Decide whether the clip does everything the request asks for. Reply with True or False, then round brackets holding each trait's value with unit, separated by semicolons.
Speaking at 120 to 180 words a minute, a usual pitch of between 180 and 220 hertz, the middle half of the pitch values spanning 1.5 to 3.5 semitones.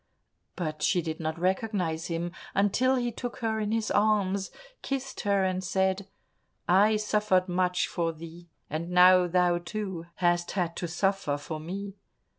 True (155 wpm; 185 Hz; 2.9 semitones)